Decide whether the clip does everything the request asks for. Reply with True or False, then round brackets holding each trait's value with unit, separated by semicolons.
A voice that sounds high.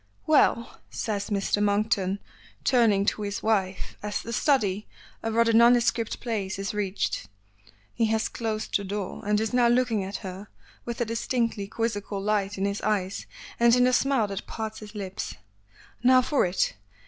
True (215 Hz)